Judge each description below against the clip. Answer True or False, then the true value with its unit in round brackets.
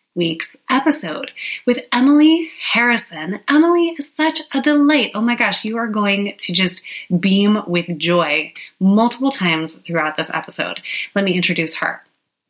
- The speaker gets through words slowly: False (145 wpm)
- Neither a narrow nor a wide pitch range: False (7.6 semitones)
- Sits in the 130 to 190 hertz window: False (205 Hz)